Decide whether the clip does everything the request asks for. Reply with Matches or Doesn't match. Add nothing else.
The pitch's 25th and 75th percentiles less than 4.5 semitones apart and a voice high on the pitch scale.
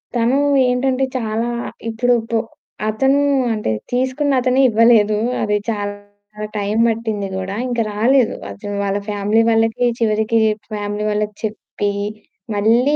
Matches